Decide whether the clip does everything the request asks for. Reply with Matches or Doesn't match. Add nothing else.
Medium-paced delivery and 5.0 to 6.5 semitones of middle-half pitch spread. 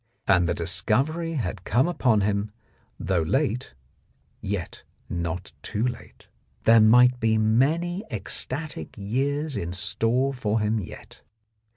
Doesn't match